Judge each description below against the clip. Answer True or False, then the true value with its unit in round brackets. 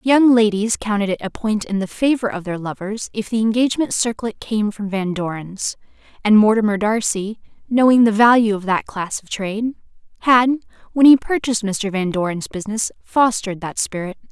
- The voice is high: True (215 Hz)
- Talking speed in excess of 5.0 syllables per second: True (5.3 syllables/s)